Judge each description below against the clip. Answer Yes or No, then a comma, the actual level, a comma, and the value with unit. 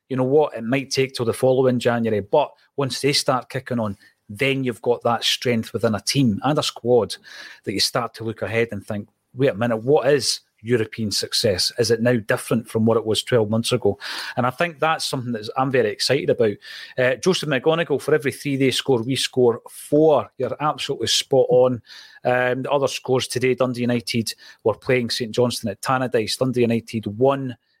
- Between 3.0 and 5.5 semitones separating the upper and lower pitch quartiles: No, narrow, 2.5 semitones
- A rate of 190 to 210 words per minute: Yes, fast, 205 wpm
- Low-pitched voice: Yes, low, 125 Hz